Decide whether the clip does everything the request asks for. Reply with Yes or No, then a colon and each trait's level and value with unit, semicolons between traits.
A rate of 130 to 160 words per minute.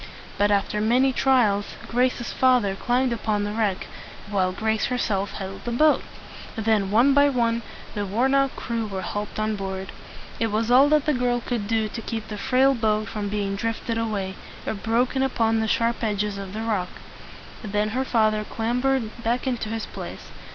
No: average, 185 wpm